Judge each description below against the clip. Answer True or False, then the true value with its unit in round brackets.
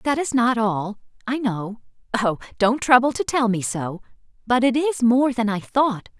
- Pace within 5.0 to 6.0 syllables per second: False (4.4 syllables/s)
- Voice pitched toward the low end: False (230 Hz)